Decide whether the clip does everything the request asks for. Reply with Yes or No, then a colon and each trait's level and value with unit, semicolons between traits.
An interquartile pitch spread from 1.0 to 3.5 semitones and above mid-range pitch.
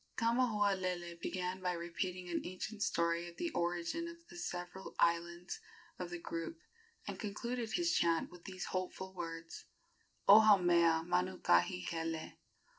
No: narrow, 2.5 semitones; medium, 180 Hz